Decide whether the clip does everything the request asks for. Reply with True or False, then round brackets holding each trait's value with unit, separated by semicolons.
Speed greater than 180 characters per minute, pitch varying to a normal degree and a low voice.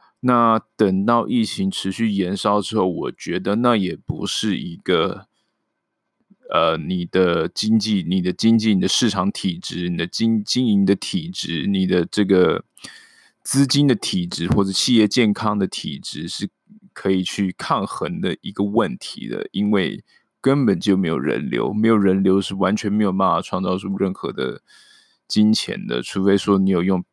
True (240 characters per minute; 4.1 semitones; 105 Hz)